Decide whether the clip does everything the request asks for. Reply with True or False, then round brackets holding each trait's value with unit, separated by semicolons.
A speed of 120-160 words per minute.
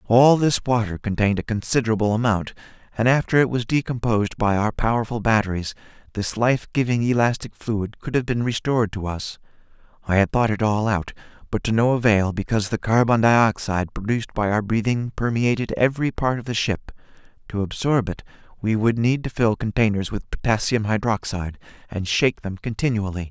False (175 wpm)